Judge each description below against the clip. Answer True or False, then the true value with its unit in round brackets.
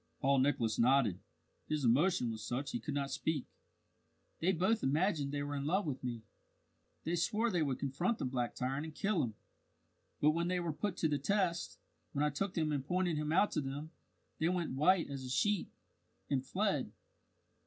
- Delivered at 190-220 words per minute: True (195 wpm)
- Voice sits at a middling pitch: True (150 Hz)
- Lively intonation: False (4.7 semitones)